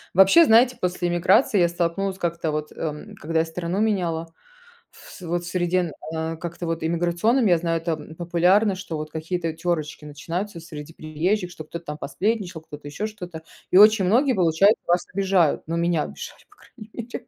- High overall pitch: No, medium, 175 Hz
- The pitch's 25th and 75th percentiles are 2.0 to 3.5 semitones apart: Yes, average, 3.1 semitones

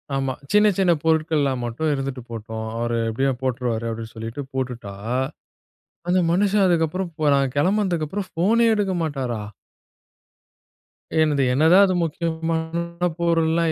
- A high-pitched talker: No, medium, 155 Hz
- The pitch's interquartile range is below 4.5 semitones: No, average, 5.2 semitones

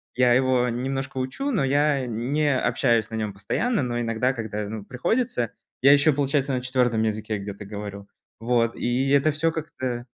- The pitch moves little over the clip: No, average, 3.6 semitones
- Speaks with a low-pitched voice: Yes, low, 125 Hz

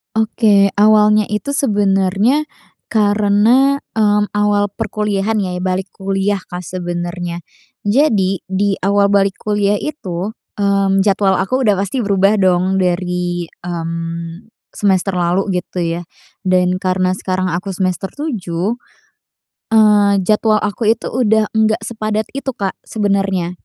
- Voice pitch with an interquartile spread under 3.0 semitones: Yes, narrow, 2.5 semitones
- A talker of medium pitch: No, high, 200 Hz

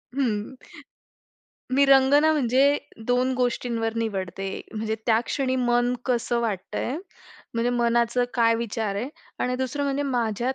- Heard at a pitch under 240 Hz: No, high, 245 Hz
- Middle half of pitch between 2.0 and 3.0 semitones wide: Yes, narrow, 2.4 semitones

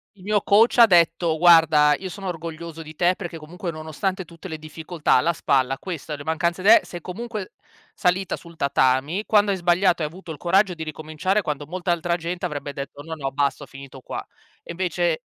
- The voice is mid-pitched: Yes, medium, 170 Hz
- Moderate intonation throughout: Yes, average, 3.1 semitones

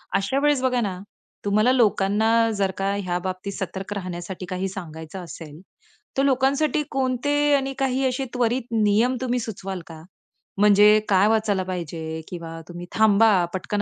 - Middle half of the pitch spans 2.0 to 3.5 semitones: No, average, 5.1 semitones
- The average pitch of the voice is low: No, high, 205 Hz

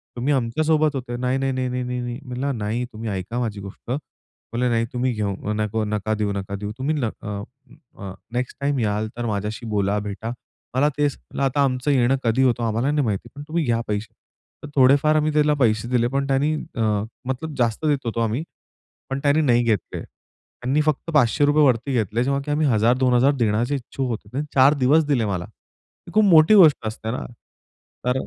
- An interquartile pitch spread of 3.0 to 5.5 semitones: Yes, average, 4.2 semitones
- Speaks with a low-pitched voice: Yes, low, 125 Hz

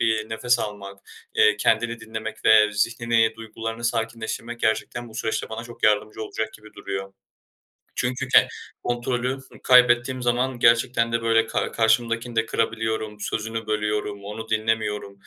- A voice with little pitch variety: Yes, narrow, 1.5 semitones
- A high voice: No, low, 115 Hz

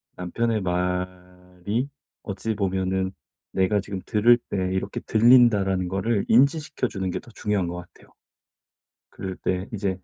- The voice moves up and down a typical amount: Yes, average, 3.0 semitones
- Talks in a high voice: No, very low, 95 Hz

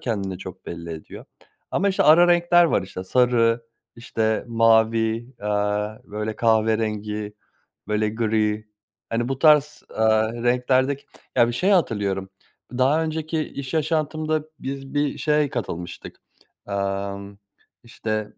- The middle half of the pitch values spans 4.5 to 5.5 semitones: Yes, average, 5.1 semitones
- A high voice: No, low, 115 Hz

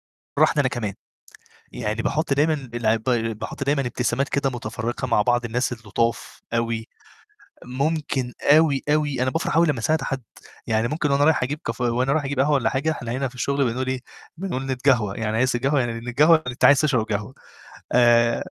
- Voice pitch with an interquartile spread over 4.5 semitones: No, average, 3.3 semitones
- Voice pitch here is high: No, low, 130 Hz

